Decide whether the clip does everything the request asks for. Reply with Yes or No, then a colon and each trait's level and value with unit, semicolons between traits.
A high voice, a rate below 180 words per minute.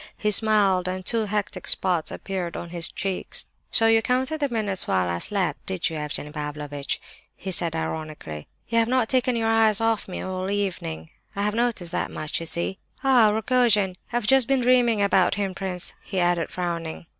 No: high, 195 Hz; average, 190 wpm